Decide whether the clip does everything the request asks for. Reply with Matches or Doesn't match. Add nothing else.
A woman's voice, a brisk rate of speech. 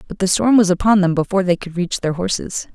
Matches